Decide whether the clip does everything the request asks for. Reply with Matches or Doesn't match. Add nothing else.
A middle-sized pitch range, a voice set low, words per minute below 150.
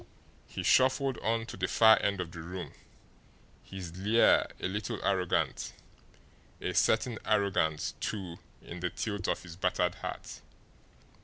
Matches